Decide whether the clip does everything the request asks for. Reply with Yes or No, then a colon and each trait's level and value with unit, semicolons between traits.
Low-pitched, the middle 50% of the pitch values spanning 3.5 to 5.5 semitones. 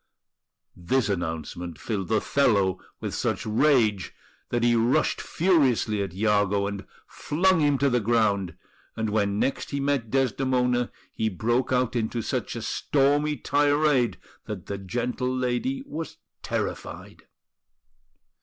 Yes: low, 120 Hz; average, 5.2 semitones